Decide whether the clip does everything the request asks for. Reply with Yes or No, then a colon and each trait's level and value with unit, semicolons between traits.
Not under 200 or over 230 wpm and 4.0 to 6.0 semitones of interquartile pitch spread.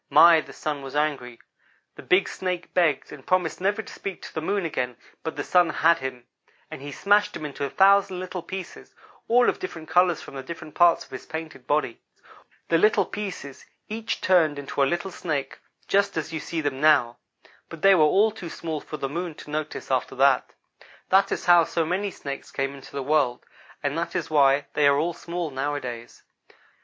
Yes: fast, 205 wpm; average, 4.3 semitones